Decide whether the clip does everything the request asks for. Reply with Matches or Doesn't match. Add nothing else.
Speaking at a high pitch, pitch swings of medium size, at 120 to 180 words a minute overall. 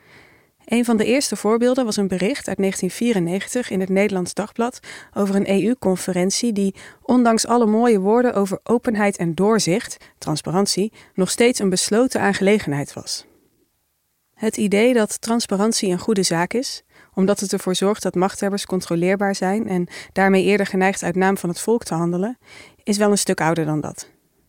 Matches